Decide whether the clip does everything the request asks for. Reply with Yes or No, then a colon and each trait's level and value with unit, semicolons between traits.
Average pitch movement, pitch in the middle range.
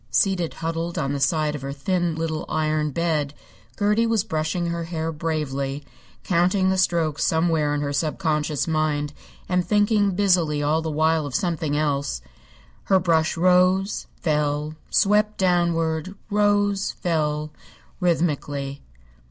Yes: average, 3.2 semitones; medium, 160 Hz